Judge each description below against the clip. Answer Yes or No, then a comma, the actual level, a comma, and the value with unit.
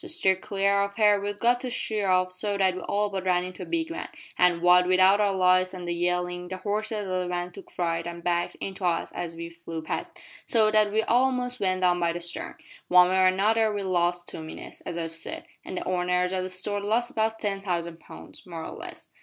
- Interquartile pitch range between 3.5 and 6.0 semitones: No, narrow, 2.6 semitones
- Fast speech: Yes, fast, 240 wpm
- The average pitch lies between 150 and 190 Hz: Yes, medium, 185 Hz